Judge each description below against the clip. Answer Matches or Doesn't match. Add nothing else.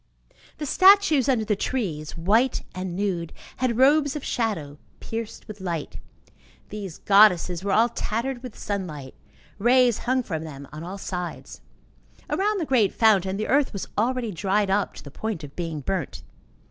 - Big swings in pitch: Matches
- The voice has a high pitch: Matches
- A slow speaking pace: Doesn't match